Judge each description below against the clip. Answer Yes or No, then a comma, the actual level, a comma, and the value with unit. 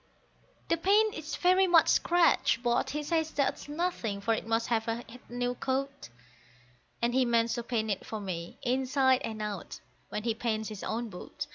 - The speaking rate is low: No, average, 185 wpm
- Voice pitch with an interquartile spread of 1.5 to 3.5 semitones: No, average, 4.9 semitones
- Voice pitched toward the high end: Yes, high, 240 Hz